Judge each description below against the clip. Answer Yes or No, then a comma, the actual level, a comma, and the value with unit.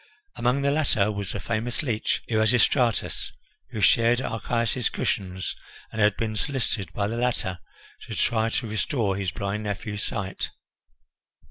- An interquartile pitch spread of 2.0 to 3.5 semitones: Yes, average, 2.9 semitones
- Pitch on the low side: Yes, low, 110 Hz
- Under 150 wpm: Yes, average, 140 wpm